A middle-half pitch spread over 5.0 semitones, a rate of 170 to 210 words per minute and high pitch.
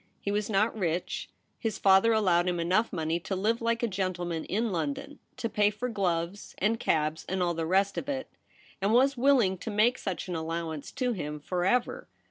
No: average, 4.7 semitones; average, 200 wpm; high, 195 Hz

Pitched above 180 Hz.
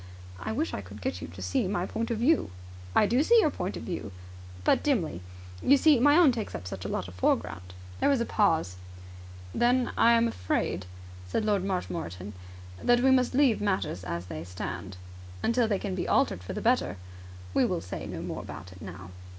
Yes: high, 190 Hz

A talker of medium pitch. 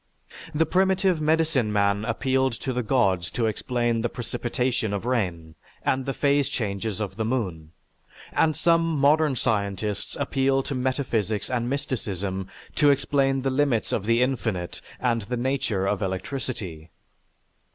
No: low, 120 Hz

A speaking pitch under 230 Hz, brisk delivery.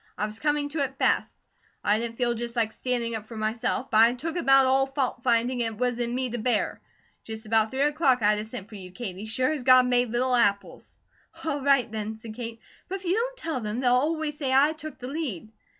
No: high, 245 Hz; fast, 235 wpm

